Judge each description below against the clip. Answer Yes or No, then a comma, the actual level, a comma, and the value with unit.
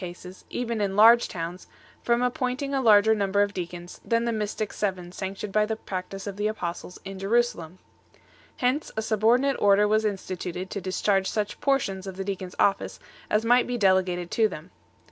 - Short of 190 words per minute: No, average, 195 wpm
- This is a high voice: Yes, high, 205 Hz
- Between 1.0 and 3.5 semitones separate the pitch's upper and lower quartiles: Yes, average, 3.2 semitones